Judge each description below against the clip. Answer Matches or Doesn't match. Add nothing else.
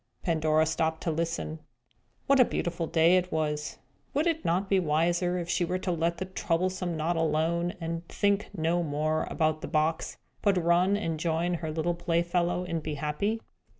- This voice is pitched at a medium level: Matches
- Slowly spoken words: Doesn't match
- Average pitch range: Doesn't match